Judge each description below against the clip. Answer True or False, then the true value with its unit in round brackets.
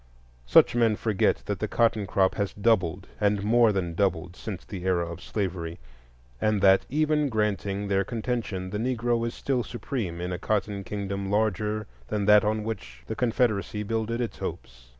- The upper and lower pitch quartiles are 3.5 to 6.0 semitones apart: False (2.9 semitones)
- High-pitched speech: False (105 Hz)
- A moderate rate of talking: True (170 wpm)